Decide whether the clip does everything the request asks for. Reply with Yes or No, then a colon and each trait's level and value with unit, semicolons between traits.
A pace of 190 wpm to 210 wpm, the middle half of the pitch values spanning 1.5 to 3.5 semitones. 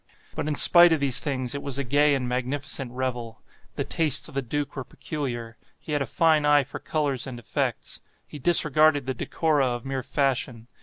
Yes: average, 200 wpm; average, 2.8 semitones